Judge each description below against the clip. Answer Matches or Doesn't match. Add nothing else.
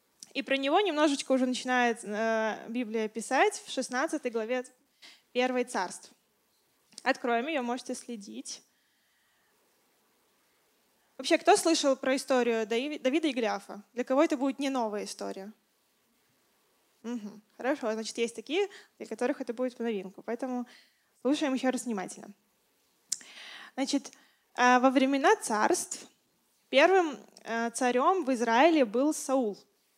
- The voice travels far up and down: Doesn't match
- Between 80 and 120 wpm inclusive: Matches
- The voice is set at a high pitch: Matches